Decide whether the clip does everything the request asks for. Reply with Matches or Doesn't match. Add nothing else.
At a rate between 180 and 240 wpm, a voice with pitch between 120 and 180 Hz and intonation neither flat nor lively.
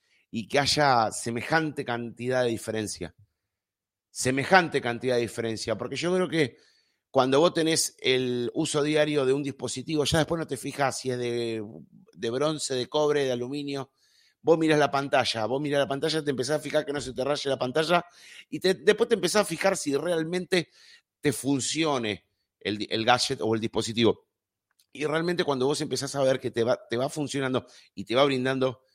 Matches